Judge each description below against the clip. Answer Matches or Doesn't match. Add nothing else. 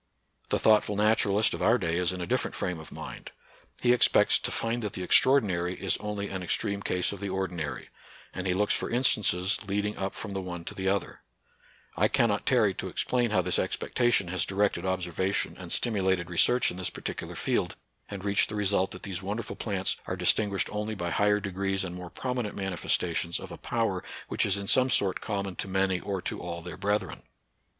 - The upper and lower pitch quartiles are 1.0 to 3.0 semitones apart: Matches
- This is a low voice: Matches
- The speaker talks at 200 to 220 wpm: Matches